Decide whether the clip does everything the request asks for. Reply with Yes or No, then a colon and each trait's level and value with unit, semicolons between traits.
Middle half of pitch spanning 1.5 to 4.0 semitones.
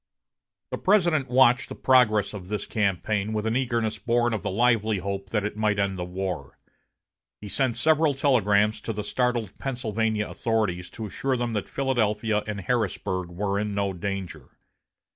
Yes: average, 3.4 semitones